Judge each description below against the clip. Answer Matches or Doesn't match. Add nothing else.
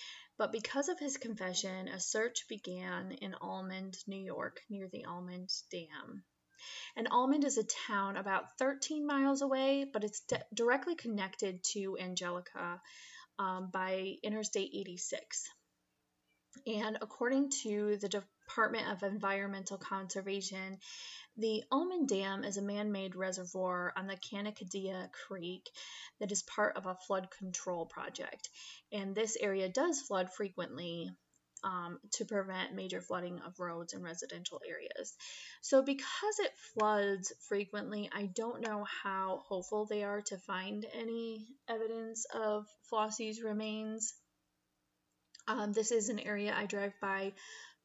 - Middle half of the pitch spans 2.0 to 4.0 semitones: Matches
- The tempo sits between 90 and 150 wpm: Matches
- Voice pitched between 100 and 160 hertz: Doesn't match